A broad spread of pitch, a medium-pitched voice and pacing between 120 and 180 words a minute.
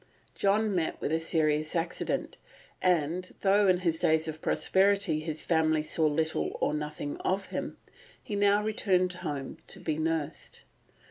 No: average, 3.4 semitones; medium, 165 Hz; average, 150 wpm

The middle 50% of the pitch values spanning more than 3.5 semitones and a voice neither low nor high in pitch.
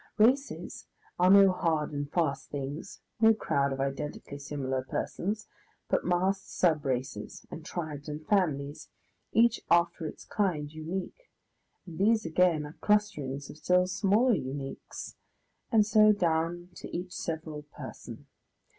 Yes: average, 5.2 semitones; medium, 165 Hz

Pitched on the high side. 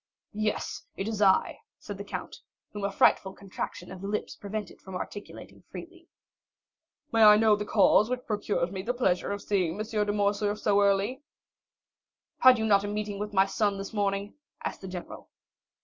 Yes: high, 205 Hz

